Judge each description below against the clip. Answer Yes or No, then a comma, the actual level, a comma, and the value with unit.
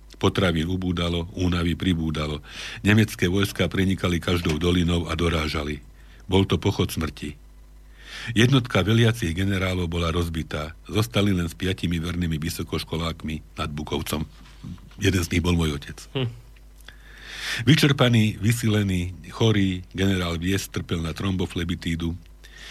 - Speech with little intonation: No, average, 3.0 semitones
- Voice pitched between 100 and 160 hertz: No, very low, 90 Hz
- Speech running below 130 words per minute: Yes, slow, 110 wpm